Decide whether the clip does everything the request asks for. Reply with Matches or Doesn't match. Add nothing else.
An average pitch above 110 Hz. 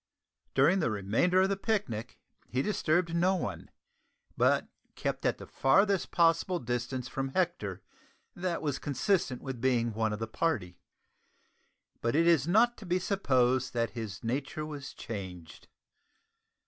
Matches